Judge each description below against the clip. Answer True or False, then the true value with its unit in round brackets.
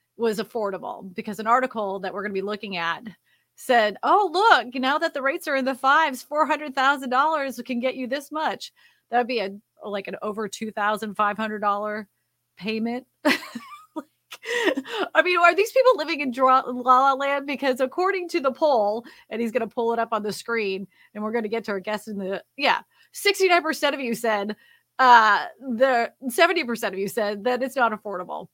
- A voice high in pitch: True (245 Hz)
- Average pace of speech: False (210 wpm)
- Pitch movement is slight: False (5.2 semitones)